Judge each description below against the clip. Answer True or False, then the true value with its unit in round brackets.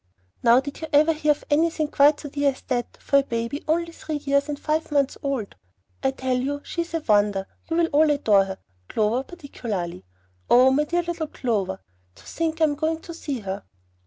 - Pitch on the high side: True (285 Hz)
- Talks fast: True (210 wpm)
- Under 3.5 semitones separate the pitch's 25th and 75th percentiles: False (4.7 semitones)